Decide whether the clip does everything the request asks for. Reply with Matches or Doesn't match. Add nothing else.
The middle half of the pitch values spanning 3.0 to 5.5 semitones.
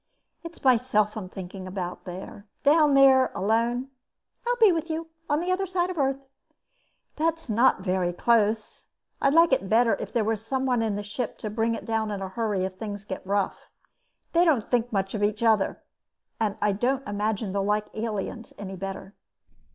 Matches